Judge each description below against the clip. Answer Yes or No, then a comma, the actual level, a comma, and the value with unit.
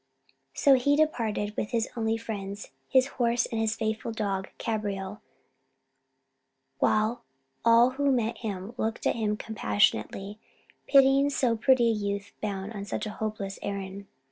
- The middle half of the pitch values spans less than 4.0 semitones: Yes, average, 2.8 semitones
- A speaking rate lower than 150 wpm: Yes, average, 140 wpm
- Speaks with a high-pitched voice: Yes, high, 220 Hz